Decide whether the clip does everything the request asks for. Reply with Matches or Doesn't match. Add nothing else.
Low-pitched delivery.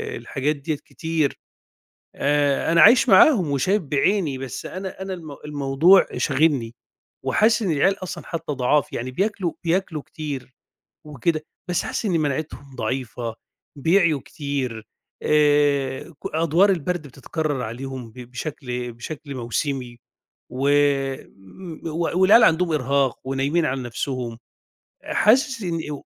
Doesn't match